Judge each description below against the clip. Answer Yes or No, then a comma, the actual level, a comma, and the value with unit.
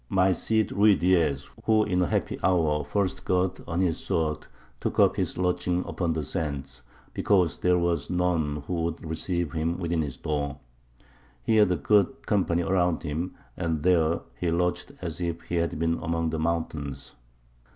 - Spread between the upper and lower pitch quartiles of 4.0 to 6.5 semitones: No, narrow, 2.5 semitones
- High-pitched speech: No, very low, 85 Hz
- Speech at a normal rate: Yes, average, 175 wpm